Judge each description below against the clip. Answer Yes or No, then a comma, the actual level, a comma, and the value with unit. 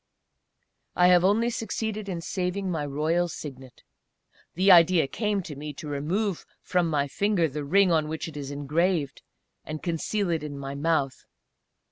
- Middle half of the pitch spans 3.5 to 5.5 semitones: Yes, average, 4.2 semitones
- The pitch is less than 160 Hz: No, medium, 165 Hz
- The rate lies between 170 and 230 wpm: No, average, 160 wpm